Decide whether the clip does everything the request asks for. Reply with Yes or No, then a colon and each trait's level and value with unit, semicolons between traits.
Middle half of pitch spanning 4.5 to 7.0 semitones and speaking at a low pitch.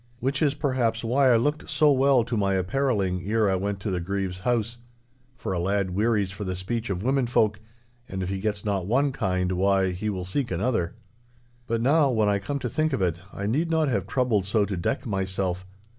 Yes: average, 5.1 semitones; low, 105 Hz